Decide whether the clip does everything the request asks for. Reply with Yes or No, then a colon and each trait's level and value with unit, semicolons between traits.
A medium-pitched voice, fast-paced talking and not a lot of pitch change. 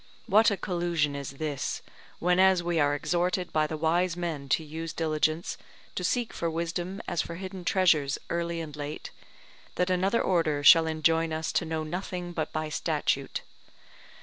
No: medium, 165 Hz; average, 165 wpm; narrow, 2.3 semitones